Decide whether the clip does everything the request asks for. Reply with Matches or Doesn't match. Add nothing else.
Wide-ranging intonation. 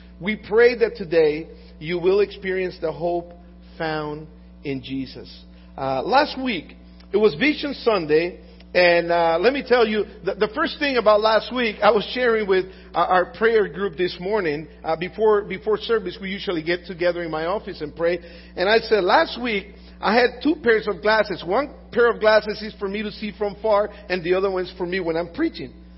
Doesn't match